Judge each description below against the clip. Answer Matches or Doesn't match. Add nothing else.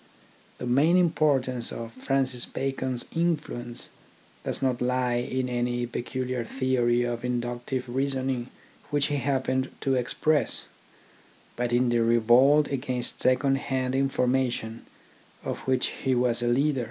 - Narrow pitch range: Matches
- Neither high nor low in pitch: Doesn't match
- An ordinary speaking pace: Doesn't match